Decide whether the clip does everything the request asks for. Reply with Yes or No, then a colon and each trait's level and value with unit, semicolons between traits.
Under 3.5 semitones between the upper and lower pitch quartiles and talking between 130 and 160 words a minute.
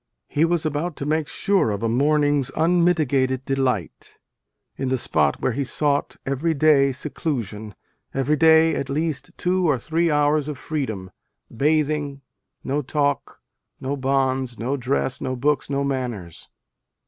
Yes: average, 2.8 semitones; average, 150 wpm